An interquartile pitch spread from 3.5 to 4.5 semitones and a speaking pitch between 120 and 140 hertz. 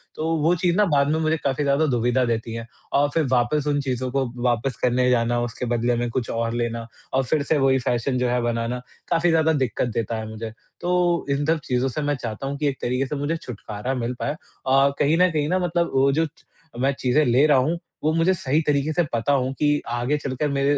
Yes: average, 3.8 semitones; low, 135 Hz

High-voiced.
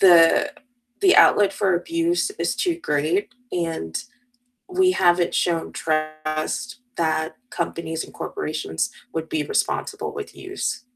No: medium, 175 Hz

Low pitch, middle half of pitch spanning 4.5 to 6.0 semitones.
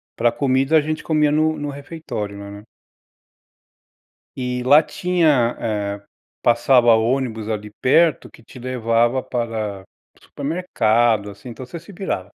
Yes: low, 125 Hz; average, 4.8 semitones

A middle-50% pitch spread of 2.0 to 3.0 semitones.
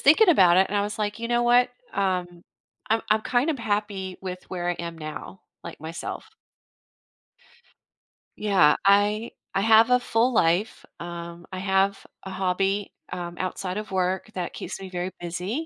No: average, 3.5 semitones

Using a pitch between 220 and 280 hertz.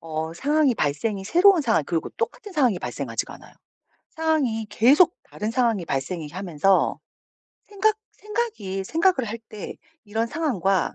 Yes: high, 225 Hz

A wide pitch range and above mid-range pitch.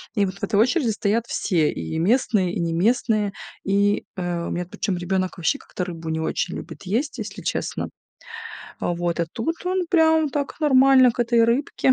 Yes: wide, 6.5 semitones; high, 205 Hz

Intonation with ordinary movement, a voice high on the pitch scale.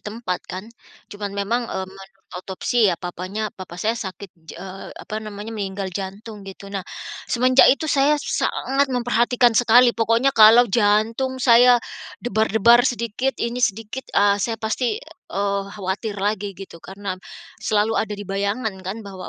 Yes: average, 3.2 semitones; high, 215 Hz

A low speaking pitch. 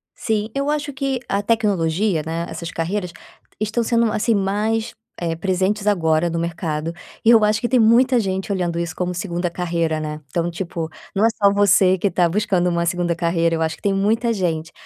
No: medium, 185 Hz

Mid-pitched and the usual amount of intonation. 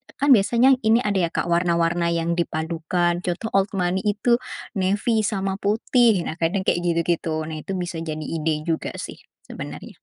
Yes: medium, 175 Hz; average, 3.6 semitones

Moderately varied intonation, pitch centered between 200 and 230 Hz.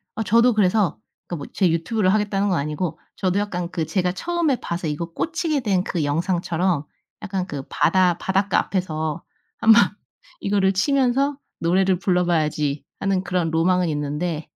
No: average, 3.7 semitones; medium, 185 Hz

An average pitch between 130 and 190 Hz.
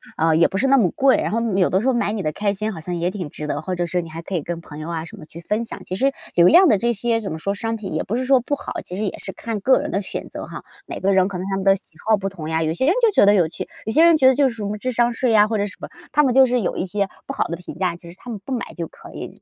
No: high, 200 Hz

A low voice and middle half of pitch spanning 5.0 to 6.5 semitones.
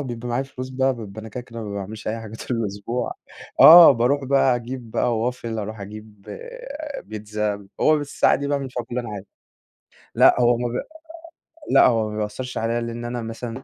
No: low, 115 Hz; average, 2.8 semitones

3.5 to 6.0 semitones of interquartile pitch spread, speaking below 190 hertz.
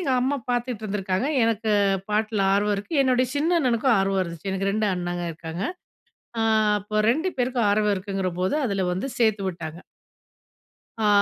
No: average, 4.2 semitones; high, 210 Hz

